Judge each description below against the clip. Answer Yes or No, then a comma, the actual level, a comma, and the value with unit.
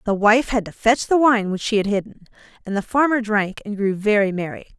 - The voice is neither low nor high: No, high, 215 Hz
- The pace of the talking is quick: Yes, fast, 240 wpm